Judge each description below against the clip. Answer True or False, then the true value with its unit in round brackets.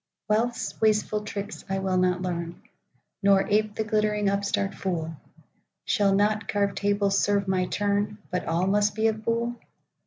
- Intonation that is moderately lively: False (1.7 semitones)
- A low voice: False (205 Hz)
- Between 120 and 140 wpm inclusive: True (135 wpm)